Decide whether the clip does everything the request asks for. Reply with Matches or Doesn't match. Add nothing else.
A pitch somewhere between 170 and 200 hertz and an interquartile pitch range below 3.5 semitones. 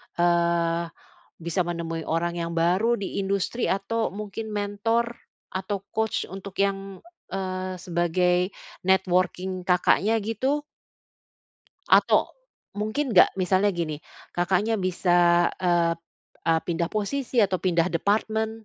Matches